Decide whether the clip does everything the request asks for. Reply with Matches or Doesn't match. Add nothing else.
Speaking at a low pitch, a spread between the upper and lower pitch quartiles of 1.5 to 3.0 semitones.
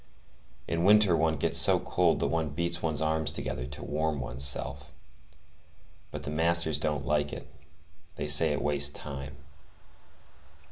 Matches